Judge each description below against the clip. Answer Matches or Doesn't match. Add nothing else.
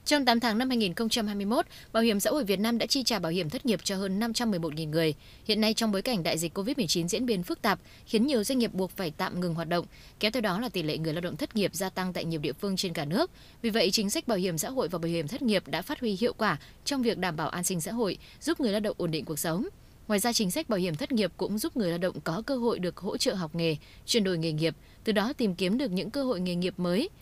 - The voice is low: Doesn't match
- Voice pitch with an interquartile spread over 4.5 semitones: Matches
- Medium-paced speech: Doesn't match